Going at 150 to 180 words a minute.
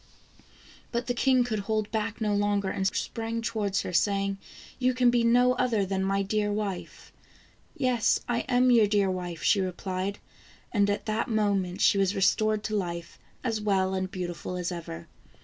No: average, 190 wpm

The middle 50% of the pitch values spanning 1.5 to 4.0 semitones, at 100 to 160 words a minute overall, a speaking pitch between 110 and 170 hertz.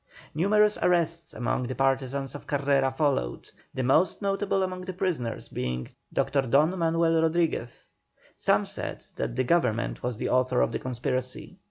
No: average, 5.1 semitones; average, 155 wpm; medium, 140 Hz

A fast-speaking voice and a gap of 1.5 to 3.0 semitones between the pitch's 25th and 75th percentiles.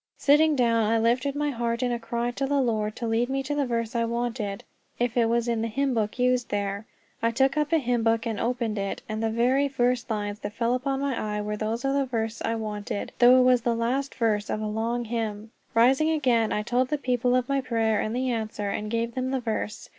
Yes: fast, 245 wpm; narrow, 2.4 semitones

